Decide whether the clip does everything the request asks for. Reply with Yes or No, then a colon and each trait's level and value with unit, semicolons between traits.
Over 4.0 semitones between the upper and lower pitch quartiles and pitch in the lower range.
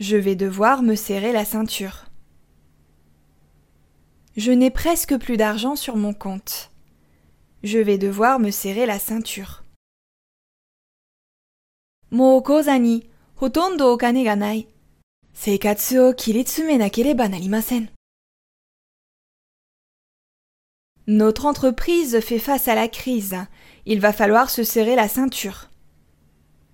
No: average, 5.3 semitones; high, 215 Hz